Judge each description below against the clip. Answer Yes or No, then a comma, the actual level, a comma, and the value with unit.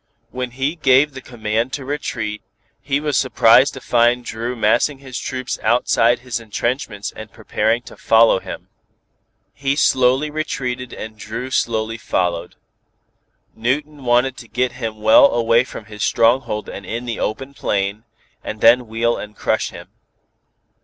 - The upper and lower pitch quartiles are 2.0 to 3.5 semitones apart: Yes, average, 3.0 semitones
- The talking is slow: No, average, 155 wpm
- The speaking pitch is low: Yes, low, 120 Hz